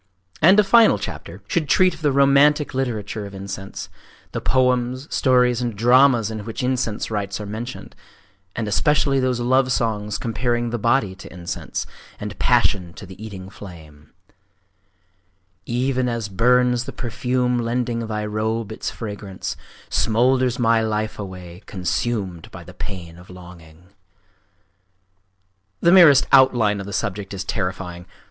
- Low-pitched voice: Yes, low, 115 Hz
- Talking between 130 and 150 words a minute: Yes, average, 140 wpm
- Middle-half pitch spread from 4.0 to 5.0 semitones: Yes, average, 4.4 semitones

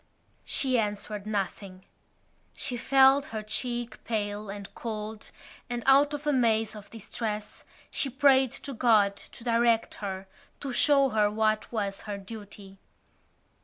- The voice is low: No, high, 220 Hz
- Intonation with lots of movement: No, average, 3.2 semitones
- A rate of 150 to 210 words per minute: No, slow, 135 wpm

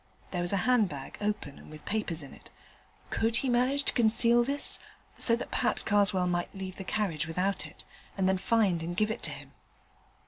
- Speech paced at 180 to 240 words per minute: Yes, average, 200 wpm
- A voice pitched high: Yes, high, 195 Hz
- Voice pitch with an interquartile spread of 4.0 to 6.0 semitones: Yes, average, 4.7 semitones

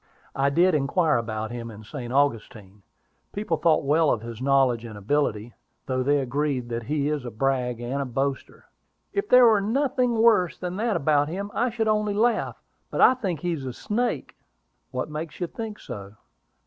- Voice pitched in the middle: Yes, medium, 145 Hz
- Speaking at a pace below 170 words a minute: No, average, 185 wpm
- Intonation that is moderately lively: No, wide, 8.5 semitones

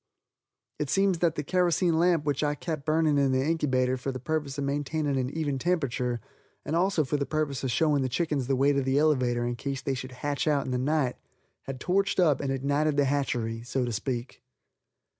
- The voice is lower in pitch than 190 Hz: Yes, medium, 140 Hz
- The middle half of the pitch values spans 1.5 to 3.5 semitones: Yes, average, 3.1 semitones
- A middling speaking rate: No, fast, 215 wpm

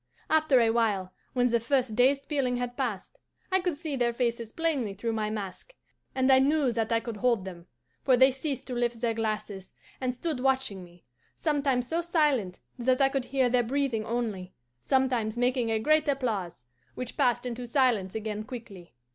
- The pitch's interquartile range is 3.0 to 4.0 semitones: Yes, average, 3.4 semitones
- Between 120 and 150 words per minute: No, average, 185 wpm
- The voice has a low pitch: No, high, 245 Hz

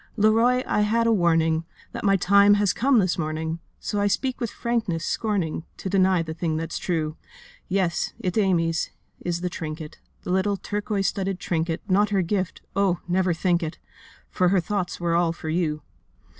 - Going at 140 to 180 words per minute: Yes, average, 170 wpm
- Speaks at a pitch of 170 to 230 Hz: Yes, medium, 185 Hz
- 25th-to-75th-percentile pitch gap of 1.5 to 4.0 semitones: Yes, average, 3.6 semitones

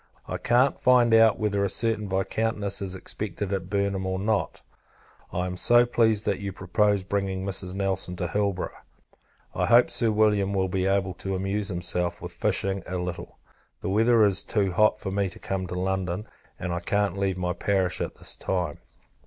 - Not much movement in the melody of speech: Yes, narrow, 2.1 semitones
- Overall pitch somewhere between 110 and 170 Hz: No, very low, 95 Hz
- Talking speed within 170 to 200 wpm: Yes, average, 185 wpm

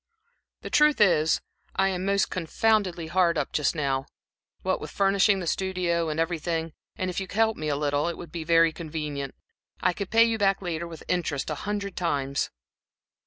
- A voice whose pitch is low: No, medium, 170 Hz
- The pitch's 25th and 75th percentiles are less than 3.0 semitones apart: No, average, 3.7 semitones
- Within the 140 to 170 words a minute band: No, average, 190 wpm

